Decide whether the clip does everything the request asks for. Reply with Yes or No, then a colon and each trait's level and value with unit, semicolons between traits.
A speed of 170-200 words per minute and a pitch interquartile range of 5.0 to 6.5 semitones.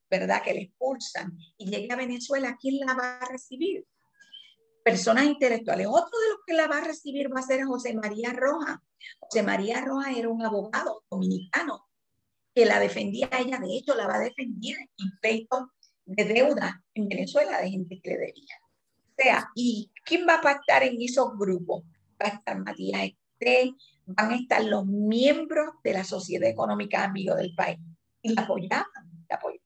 Yes: average, 180 wpm; wide, 5.5 semitones